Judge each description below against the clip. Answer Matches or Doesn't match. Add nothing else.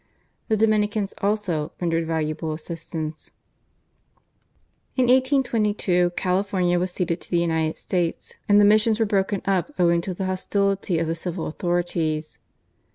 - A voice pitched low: Doesn't match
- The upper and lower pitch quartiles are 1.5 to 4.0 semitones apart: Matches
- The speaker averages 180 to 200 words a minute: Doesn't match